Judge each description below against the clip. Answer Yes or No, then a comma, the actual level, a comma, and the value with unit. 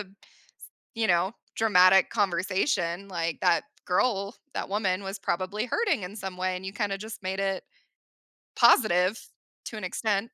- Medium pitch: No, high, 195 Hz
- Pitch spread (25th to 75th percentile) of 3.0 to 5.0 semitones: No, narrow, 2.4 semitones